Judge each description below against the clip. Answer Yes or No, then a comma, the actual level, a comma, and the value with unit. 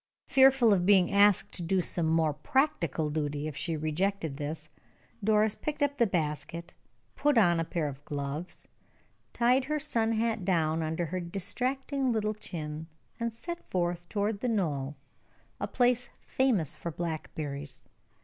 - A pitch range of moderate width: No, wide, 6.6 semitones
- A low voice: No, medium, 180 Hz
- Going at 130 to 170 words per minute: Yes, average, 150 wpm